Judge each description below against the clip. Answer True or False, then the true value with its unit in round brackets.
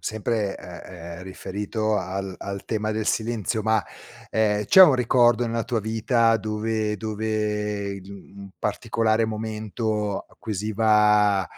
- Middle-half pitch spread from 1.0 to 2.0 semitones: True (1.5 semitones)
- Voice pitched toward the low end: True (110 Hz)